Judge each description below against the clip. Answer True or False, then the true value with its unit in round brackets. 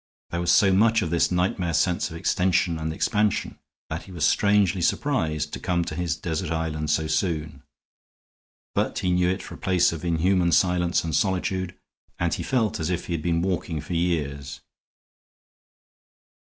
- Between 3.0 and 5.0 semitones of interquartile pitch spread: False (2.4 semitones)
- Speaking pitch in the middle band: False (85 Hz)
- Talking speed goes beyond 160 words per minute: True (175 wpm)